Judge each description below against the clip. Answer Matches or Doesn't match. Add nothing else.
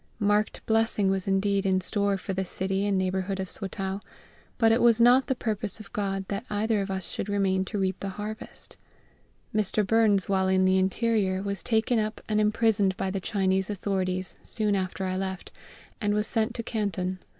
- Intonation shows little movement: Matches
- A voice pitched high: Matches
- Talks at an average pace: Matches